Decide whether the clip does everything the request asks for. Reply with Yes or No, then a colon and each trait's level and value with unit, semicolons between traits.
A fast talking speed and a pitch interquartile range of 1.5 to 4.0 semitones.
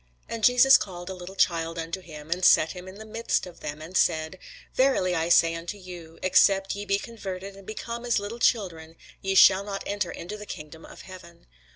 Yes: fast, 210 wpm; average, 3.4 semitones